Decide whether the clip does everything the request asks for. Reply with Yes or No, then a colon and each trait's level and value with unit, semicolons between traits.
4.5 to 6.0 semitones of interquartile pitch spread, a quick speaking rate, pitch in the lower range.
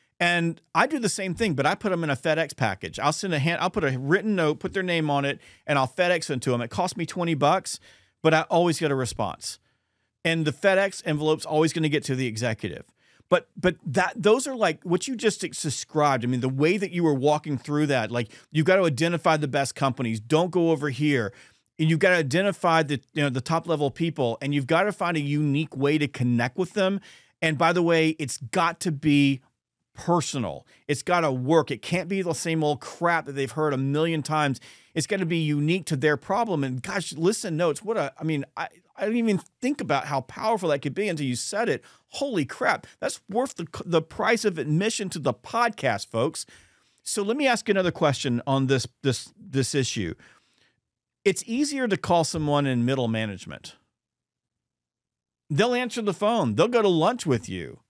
No: average, 4.8 semitones; fast, 220 wpm; medium, 160 Hz